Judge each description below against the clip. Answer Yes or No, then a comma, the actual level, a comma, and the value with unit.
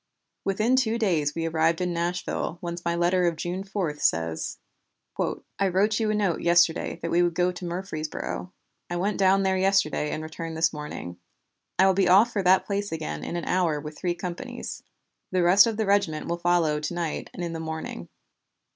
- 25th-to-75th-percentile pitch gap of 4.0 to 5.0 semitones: No, average, 3.0 semitones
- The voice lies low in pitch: No, medium, 175 Hz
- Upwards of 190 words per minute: Yes, average, 200 wpm